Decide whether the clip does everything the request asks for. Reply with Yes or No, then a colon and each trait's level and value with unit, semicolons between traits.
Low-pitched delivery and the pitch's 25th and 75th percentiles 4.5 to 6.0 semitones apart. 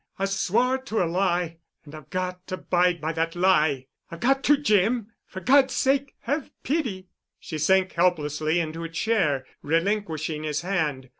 No: medium, 180 Hz; average, 5.2 semitones